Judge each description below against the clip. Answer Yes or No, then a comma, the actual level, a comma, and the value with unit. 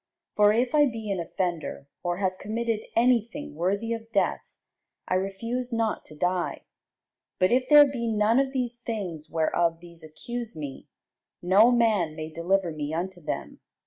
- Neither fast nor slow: Yes, average, 165 wpm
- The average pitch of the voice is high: Yes, high, 200 Hz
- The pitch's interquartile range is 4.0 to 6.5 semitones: Yes, wide, 5.4 semitones